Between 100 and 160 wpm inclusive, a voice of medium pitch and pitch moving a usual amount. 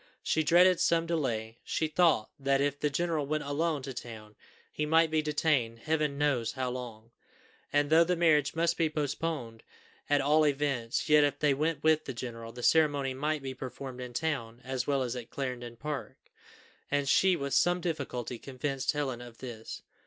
No: average, 180 wpm; medium, 145 Hz; average, 3.8 semitones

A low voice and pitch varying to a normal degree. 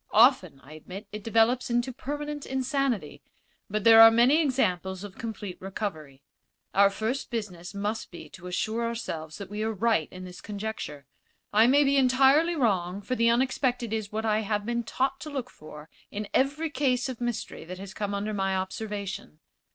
No: high, 220 Hz; average, 4.6 semitones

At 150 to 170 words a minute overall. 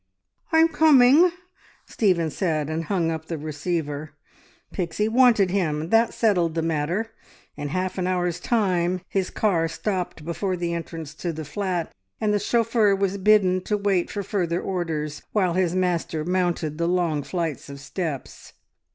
Yes: average, 155 wpm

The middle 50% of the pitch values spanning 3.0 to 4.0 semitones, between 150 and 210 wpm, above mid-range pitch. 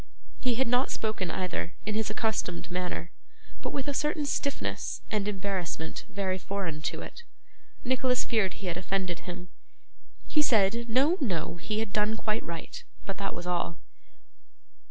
No: average, 4.7 semitones; average, 155 wpm; high, 200 Hz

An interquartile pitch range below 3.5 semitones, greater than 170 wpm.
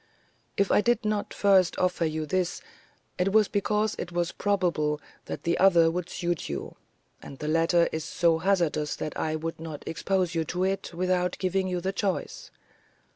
Yes: average, 2.9 semitones; average, 180 wpm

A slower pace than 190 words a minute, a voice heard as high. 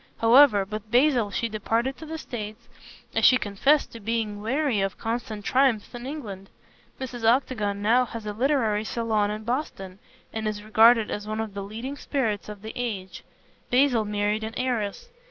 Yes: average, 175 wpm; high, 225 Hz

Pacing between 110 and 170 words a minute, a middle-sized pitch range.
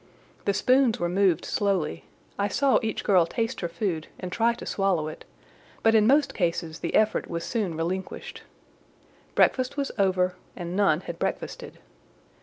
Yes: average, 160 wpm; average, 4.7 semitones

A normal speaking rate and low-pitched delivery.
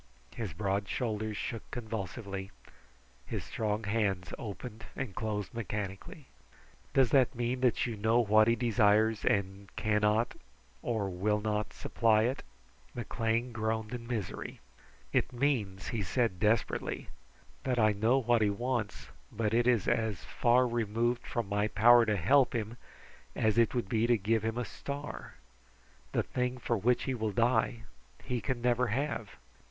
Yes: average, 150 wpm; low, 110 Hz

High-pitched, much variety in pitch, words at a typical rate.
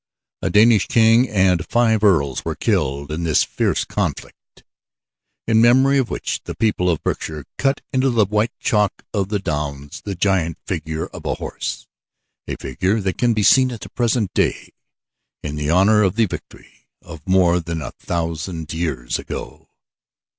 No: very low, 95 Hz; wide, 5.7 semitones; average, 165 wpm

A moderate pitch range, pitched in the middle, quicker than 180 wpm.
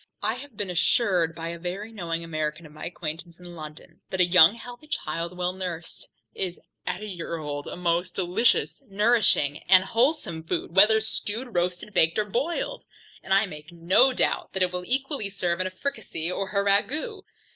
Yes: average, 4.1 semitones; medium, 180 Hz; average, 190 wpm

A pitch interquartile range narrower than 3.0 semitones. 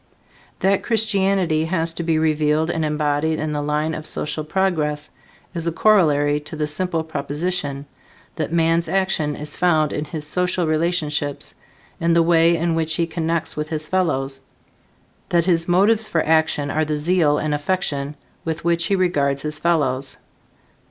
Yes: narrow, 2.4 semitones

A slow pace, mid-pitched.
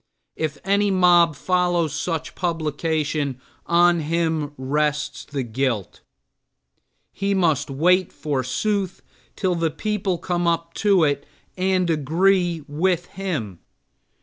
Yes: slow, 110 wpm; medium, 165 Hz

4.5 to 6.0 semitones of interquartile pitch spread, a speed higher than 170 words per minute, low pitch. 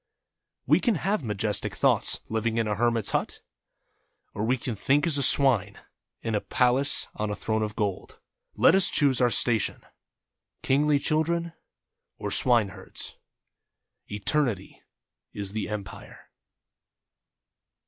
No: average, 5.0 semitones; average, 140 wpm; low, 115 Hz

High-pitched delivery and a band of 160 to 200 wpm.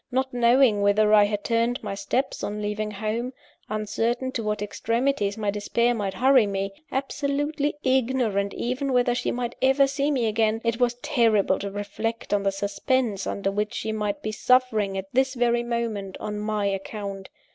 Yes: high, 225 Hz; average, 175 wpm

